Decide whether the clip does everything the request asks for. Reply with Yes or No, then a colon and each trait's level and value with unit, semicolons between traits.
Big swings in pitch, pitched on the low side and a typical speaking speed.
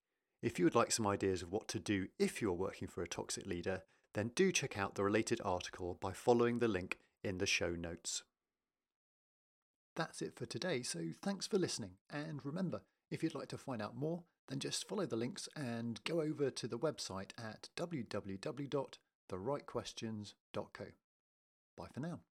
Yes: wide, 7.9 semitones; low, 120 Hz; average, 175 wpm